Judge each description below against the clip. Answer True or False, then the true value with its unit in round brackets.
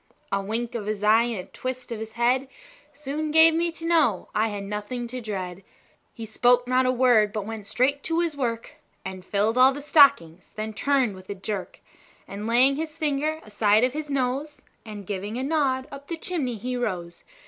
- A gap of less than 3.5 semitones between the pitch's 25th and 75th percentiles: False (4.9 semitones)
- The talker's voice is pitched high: True (240 Hz)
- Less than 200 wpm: False (205 wpm)